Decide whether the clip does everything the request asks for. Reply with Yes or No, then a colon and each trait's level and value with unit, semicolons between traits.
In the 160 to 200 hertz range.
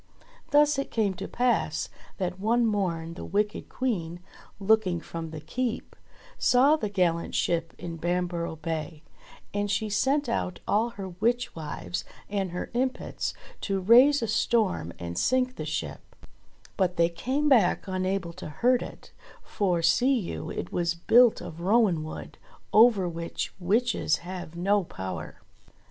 Yes: high, 190 Hz